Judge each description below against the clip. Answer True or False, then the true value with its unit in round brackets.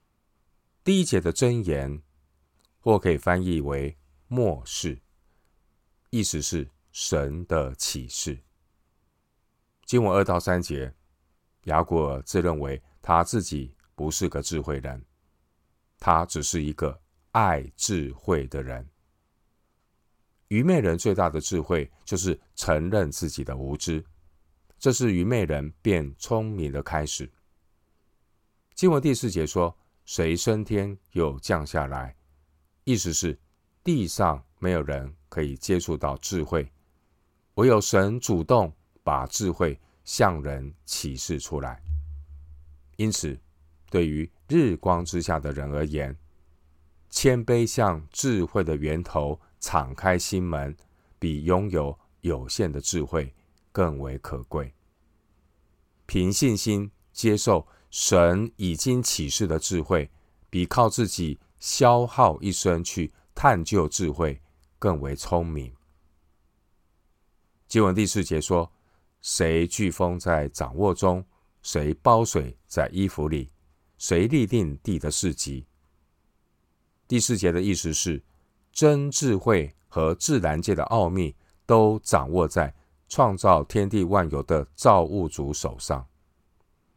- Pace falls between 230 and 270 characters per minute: False (170 characters per minute)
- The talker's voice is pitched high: False (80 Hz)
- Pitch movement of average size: True (4.1 semitones)